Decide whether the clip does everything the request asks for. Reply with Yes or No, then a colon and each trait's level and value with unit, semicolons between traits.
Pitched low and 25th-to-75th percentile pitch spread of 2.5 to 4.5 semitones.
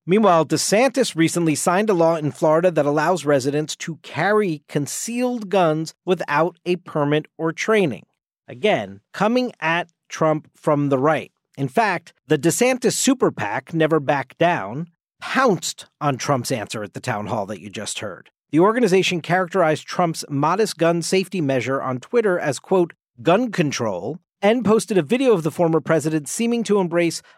No: medium, 165 Hz; average, 4.2 semitones